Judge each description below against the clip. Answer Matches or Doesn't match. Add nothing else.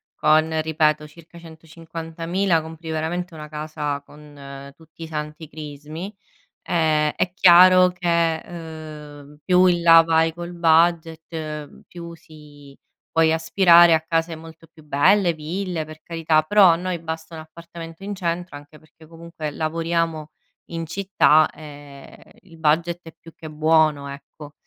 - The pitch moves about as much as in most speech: Doesn't match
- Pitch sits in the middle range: Matches